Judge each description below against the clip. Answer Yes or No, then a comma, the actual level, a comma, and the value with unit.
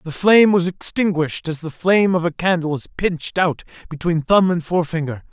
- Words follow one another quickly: No, average, 190 wpm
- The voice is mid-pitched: Yes, medium, 170 Hz